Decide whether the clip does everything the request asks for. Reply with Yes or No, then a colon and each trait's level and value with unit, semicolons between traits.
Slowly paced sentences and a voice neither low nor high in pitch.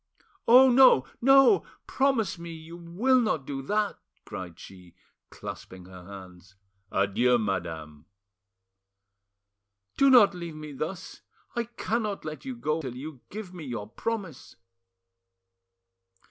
Yes: slow, 120 wpm; medium, 160 Hz